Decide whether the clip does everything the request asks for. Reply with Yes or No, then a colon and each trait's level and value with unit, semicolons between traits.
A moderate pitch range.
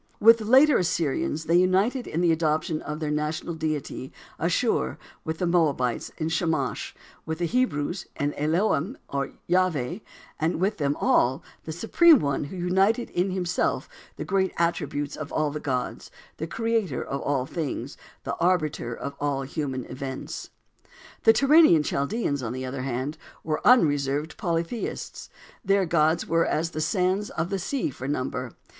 Yes: average, 4.5 semitones